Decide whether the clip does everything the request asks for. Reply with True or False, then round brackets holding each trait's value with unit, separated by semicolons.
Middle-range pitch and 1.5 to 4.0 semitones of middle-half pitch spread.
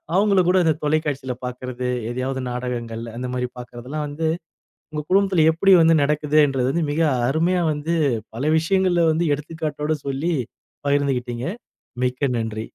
False (145 Hz; 4.4 semitones)